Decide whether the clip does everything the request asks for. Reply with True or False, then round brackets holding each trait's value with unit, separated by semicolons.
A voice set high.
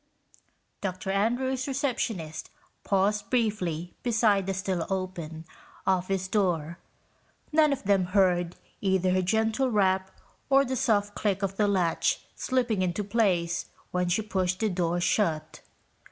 True (195 Hz)